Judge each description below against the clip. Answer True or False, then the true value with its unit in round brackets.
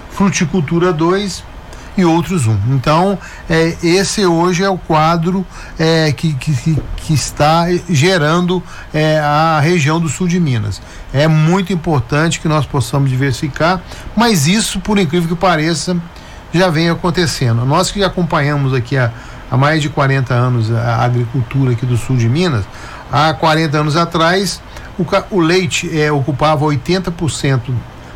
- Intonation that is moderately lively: True (4.3 semitones)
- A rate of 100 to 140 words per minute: False (150 wpm)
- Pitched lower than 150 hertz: False (160 Hz)